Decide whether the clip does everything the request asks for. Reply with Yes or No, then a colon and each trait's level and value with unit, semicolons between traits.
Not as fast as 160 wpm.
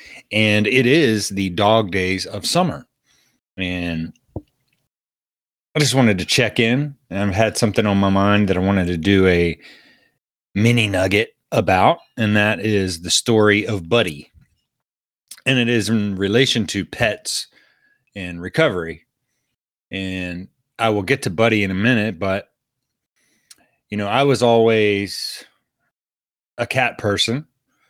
Yes: average, 140 wpm